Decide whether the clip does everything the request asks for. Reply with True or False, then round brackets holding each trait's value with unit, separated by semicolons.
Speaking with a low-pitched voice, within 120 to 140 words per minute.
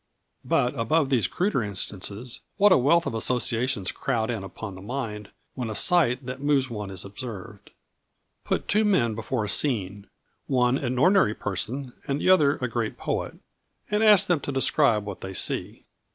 False (125 Hz; 175 wpm)